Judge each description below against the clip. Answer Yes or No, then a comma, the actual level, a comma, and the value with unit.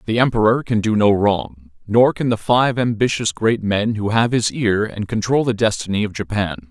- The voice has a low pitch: Yes, low, 110 Hz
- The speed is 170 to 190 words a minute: No, fast, 205 wpm